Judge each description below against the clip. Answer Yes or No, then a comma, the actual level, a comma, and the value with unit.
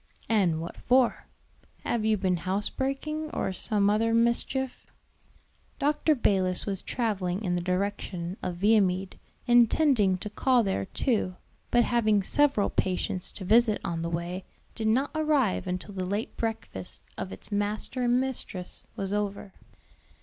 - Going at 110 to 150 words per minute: Yes, average, 145 wpm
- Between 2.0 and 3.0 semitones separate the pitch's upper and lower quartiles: No, average, 4.5 semitones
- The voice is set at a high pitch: Yes, high, 205 Hz